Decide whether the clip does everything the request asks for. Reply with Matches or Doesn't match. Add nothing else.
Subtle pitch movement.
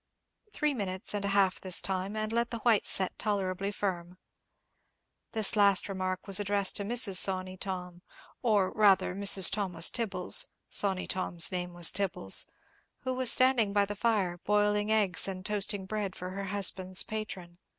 Matches